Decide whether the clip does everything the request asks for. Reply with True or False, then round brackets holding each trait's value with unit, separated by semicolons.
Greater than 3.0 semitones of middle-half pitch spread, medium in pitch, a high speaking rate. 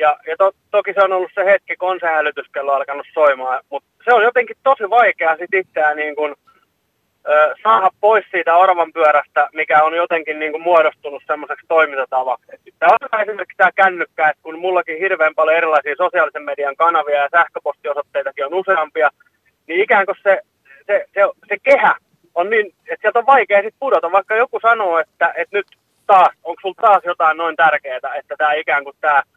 True (5.1 semitones; 170 Hz; 185 wpm)